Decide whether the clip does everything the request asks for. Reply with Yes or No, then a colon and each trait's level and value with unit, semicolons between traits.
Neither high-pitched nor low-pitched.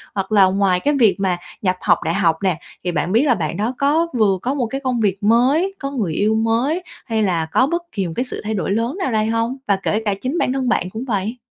No: high, 220 Hz